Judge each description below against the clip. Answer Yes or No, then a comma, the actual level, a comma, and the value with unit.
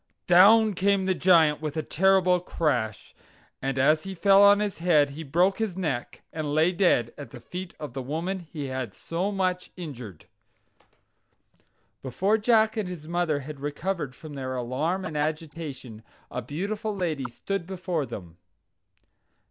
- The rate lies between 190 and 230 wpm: No, average, 155 wpm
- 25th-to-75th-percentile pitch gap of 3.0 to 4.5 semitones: No, average, 5.1 semitones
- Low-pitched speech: No, medium, 165 Hz